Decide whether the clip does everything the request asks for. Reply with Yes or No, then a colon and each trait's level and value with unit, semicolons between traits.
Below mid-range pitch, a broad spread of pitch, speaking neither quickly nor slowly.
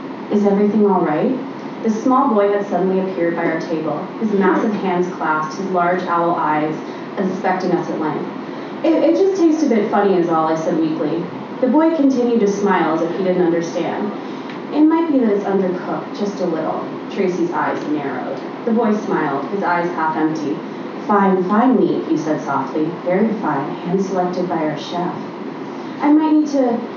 No: high, 190 Hz; wide, 6.3 semitones; average, 185 wpm